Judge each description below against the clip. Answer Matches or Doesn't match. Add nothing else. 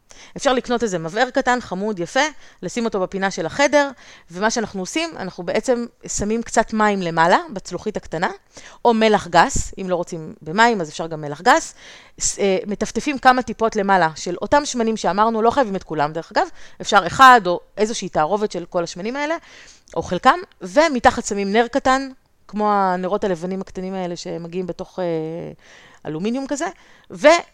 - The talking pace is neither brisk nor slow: Doesn't match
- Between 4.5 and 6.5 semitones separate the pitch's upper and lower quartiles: Matches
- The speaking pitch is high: Matches